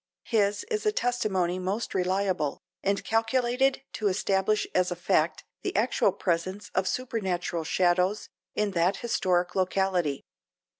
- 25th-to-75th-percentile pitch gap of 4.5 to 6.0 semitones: No, average, 3.0 semitones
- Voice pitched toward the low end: No, high, 190 Hz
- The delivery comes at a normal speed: No, slow, 130 wpm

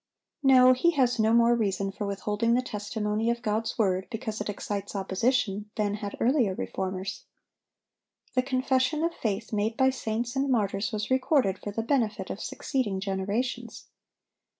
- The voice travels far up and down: No, average, 3.7 semitones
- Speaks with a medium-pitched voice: No, high, 220 Hz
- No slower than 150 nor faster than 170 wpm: Yes, average, 155 wpm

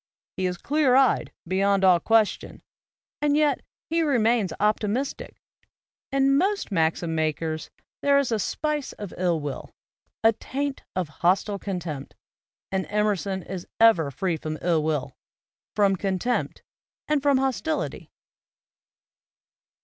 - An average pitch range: No, wide, 7.5 semitones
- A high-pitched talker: Yes, high, 200 Hz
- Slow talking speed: Yes, slow, 130 wpm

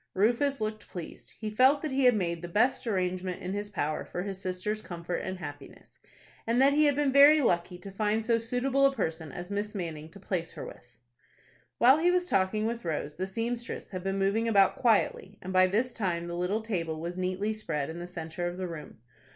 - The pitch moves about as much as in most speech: Yes, average, 4.7 semitones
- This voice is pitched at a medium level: No, high, 195 Hz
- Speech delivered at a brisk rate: Yes, fast, 215 wpm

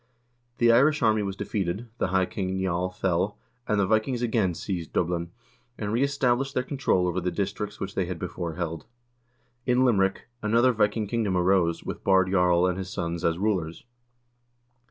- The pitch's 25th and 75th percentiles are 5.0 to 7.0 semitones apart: No, average, 3.7 semitones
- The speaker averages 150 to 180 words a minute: Yes, average, 170 wpm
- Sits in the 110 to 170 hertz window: No, very low, 95 Hz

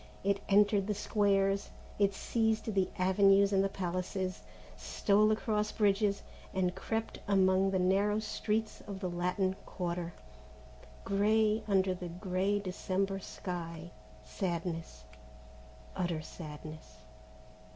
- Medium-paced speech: No, slow, 120 wpm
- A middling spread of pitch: No, narrow, 2.2 semitones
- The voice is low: No, high, 195 Hz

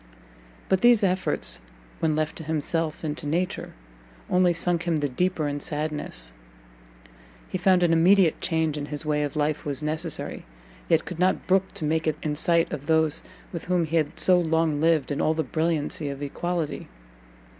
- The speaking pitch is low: No, medium, 160 Hz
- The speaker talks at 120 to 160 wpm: No, average, 180 wpm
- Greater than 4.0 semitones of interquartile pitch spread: No, average, 2.7 semitones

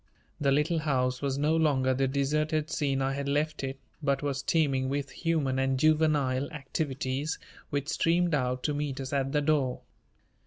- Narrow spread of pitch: Yes, narrow, 2.3 semitones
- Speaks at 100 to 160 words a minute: No, average, 170 wpm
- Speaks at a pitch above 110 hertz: Yes, medium, 140 Hz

